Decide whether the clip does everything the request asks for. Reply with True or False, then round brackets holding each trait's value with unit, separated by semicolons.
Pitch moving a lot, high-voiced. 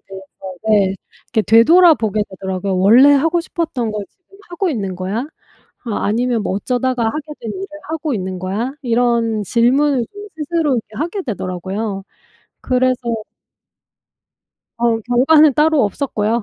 True (6.1 semitones; 235 Hz)